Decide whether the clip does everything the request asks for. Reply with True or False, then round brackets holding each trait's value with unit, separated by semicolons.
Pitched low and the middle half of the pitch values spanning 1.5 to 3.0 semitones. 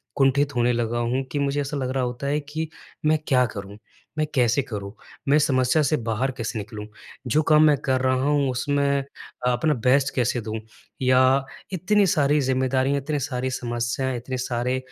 True (130 Hz; 2.7 semitones)